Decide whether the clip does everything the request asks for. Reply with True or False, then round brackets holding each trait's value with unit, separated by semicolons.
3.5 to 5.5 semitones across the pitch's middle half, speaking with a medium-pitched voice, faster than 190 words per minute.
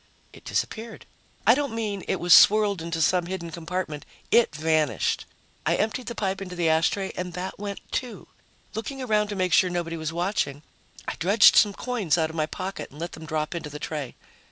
True (4.4 semitones; 180 Hz; 200 wpm)